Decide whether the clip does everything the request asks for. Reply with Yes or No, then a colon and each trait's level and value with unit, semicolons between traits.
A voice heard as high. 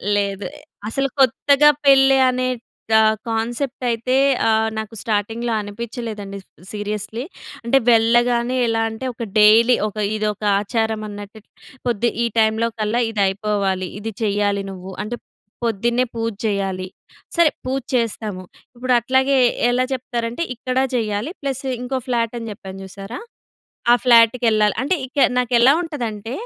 Yes: high, 230 Hz